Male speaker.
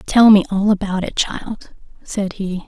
No: female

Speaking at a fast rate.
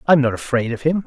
Yes: fast, 335 wpm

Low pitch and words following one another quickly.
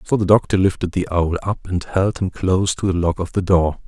Yes: very low, 90 Hz; fast, 265 wpm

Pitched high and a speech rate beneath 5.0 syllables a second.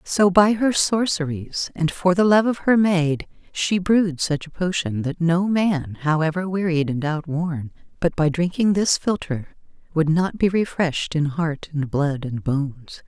No: medium, 170 Hz; 4.3 syllables/s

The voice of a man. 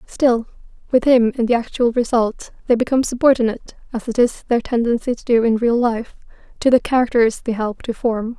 No: female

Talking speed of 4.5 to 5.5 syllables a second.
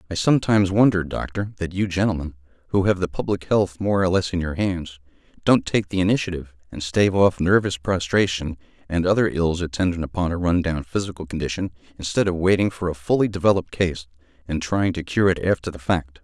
No: 6.0 syllables/s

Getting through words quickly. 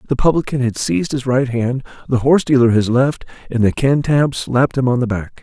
Yes: fast, 220 wpm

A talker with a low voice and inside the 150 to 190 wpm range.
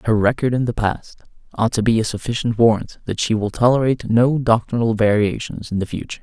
No: low, 115 Hz; average, 200 wpm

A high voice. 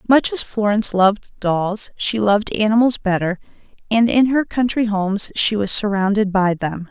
Yes: high, 210 Hz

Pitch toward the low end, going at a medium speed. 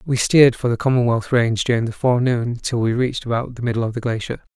No: low, 120 Hz; fast, 235 wpm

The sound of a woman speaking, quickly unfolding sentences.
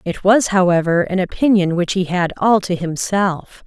No: female; average, 180 wpm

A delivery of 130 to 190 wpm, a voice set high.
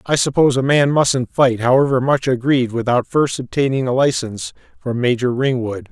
No: average, 175 wpm; low, 130 Hz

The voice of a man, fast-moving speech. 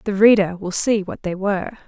No: female; fast, 225 wpm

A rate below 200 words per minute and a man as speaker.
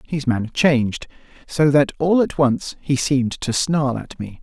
Yes: average, 175 wpm; male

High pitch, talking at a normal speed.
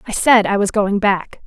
No: high, 205 Hz; fast, 245 wpm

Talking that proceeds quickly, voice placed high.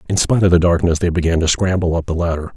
No: fast, 280 wpm; very low, 85 Hz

